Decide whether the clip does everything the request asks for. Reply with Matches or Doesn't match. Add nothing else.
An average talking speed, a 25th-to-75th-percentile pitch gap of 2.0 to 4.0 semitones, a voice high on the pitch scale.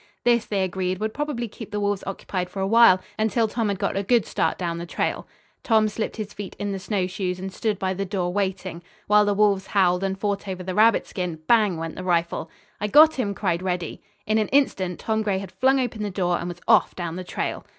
Doesn't match